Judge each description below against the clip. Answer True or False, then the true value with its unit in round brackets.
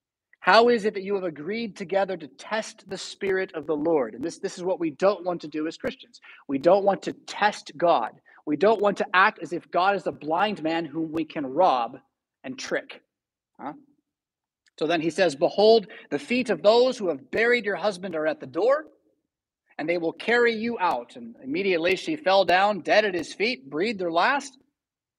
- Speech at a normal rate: False (210 wpm)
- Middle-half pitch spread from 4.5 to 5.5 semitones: True (4.8 semitones)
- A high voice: True (195 Hz)